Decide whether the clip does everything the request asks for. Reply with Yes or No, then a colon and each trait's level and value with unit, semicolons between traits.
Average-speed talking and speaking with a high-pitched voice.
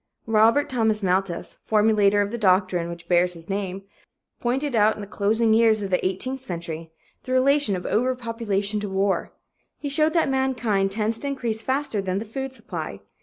Yes: average, 175 wpm; high, 215 Hz